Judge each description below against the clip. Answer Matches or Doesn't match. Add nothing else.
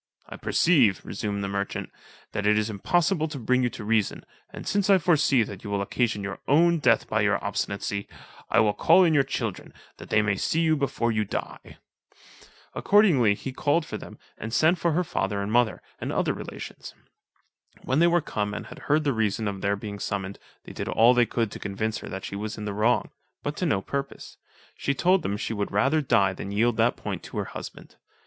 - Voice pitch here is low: Matches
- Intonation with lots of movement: Matches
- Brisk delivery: Matches